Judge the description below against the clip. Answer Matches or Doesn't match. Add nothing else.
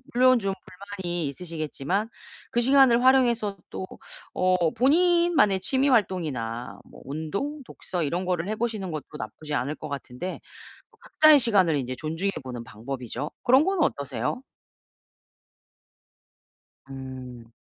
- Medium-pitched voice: Matches